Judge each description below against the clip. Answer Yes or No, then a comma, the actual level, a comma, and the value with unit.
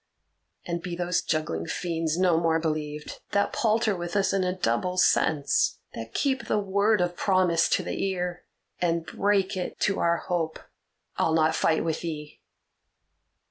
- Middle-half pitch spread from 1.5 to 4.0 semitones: Yes, average, 2.8 semitones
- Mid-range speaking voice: Yes, medium, 175 Hz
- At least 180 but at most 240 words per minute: No, average, 160 wpm